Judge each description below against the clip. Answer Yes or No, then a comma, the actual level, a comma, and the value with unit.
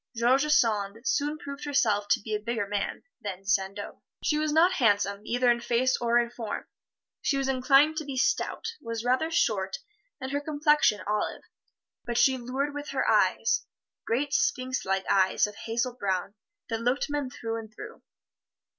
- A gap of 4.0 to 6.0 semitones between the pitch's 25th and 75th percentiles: Yes, average, 5.0 semitones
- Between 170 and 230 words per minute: Yes, average, 175 wpm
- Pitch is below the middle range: No, high, 240 Hz